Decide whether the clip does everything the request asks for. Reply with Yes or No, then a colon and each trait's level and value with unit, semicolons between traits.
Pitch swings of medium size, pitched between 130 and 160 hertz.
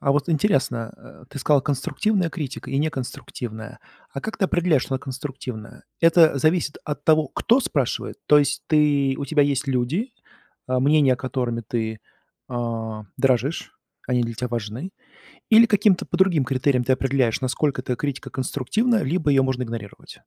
Yes: average, 3.8 semitones; low, 135 Hz